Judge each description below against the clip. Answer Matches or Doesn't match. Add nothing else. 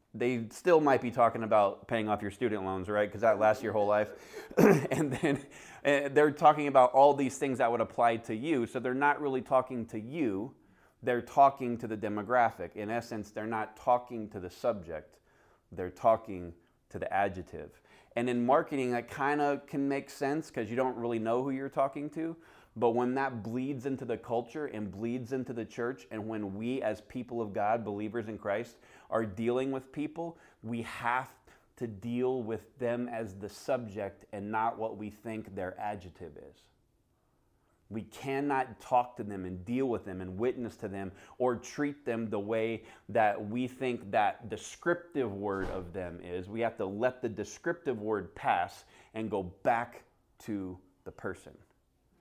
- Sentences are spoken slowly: Doesn't match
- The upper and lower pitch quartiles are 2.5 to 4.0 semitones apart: Matches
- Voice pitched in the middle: Doesn't match